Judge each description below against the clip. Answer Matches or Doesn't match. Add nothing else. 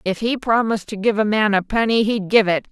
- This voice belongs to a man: Doesn't match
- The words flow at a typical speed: Doesn't match